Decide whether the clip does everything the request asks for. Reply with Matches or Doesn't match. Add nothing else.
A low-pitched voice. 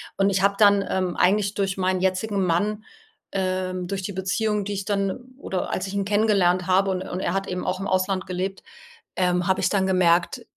Doesn't match